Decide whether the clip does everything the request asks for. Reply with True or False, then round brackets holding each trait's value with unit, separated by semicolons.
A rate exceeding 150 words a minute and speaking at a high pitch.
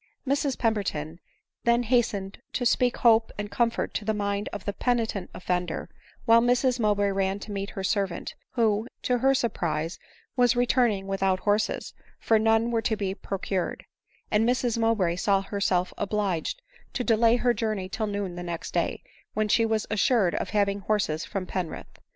True (175 wpm; 210 Hz)